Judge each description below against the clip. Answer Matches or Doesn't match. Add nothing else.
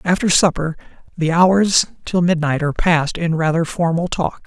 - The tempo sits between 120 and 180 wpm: Matches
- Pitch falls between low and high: Matches